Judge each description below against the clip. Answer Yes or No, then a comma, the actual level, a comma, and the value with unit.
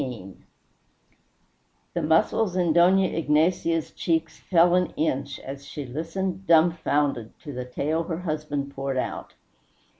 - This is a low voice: No, medium, 160 Hz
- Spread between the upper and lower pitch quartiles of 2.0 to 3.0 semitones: No, average, 3.6 semitones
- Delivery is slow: Yes, slow, 125 wpm